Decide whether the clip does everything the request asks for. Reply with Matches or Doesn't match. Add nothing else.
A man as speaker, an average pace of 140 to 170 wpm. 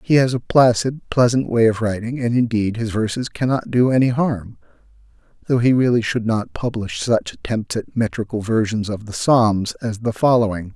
Doesn't match